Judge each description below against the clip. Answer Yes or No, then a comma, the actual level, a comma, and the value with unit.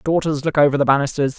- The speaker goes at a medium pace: No, fast, 215 wpm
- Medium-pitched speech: Yes, medium, 145 Hz